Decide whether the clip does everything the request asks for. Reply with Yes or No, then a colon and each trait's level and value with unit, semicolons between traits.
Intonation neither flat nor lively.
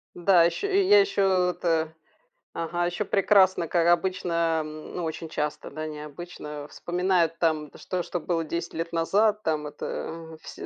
No: narrow, 2.3 semitones